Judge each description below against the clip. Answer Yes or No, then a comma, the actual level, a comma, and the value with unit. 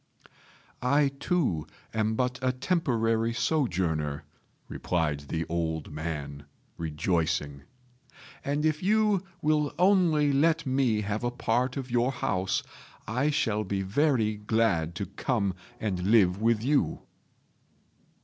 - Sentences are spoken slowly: Yes, slow, 120 wpm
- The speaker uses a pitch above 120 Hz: No, low, 115 Hz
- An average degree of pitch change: No, wide, 7.7 semitones